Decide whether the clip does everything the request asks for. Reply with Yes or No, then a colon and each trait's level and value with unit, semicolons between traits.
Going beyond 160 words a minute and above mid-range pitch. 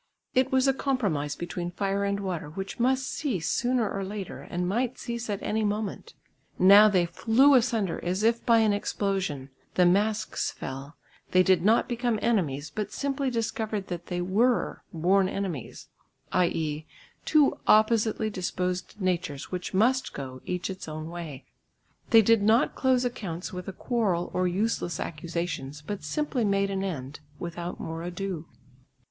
No: average, 155 wpm; high, 195 Hz